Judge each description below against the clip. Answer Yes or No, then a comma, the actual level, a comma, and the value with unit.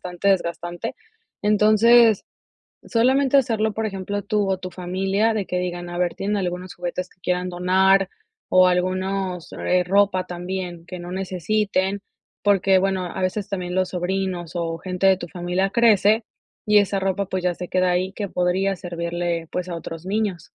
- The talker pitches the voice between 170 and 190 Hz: Yes, medium, 185 Hz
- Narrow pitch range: Yes, narrow, 2.0 semitones